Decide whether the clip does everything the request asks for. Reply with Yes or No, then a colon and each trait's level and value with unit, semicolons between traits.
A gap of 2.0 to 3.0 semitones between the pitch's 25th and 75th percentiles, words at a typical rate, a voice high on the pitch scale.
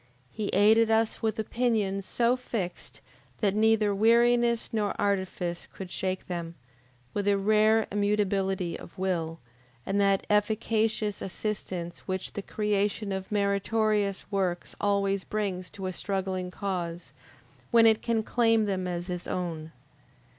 No: narrow, 2.5 semitones; slow, 130 wpm; high, 200 Hz